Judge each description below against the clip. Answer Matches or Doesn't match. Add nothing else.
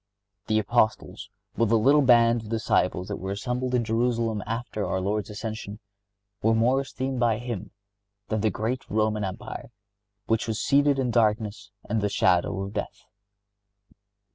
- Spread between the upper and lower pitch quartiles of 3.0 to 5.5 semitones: Doesn't match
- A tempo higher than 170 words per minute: Doesn't match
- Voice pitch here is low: Matches